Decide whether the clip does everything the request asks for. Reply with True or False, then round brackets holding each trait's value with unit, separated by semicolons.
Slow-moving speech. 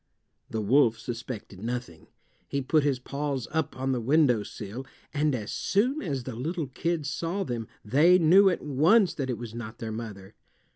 False (175 wpm)